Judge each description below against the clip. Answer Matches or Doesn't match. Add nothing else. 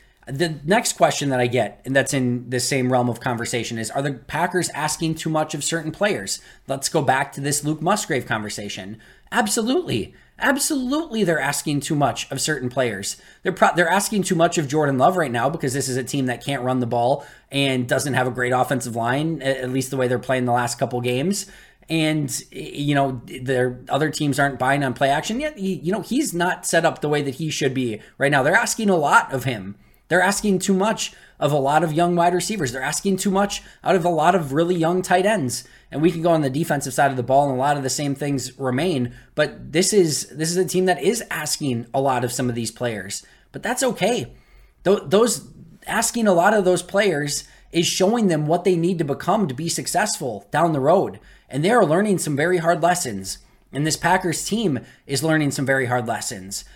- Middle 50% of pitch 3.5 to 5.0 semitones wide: Doesn't match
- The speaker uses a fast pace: Matches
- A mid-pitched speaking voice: Matches